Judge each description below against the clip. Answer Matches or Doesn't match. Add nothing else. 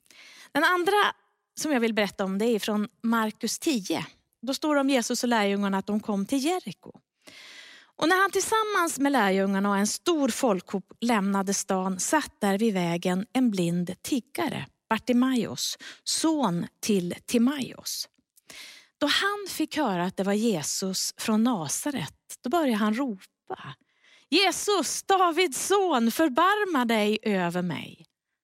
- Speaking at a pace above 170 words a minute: Doesn't match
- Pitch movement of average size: Doesn't match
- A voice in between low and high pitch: Doesn't match